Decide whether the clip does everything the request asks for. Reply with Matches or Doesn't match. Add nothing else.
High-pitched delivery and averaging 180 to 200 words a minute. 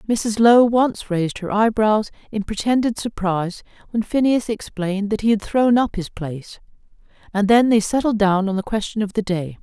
Matches